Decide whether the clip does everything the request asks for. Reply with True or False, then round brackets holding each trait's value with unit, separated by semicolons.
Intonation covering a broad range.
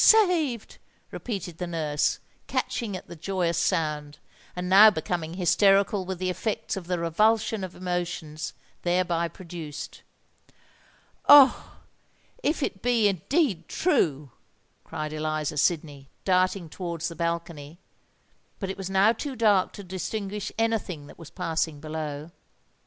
False (3.9 semitones)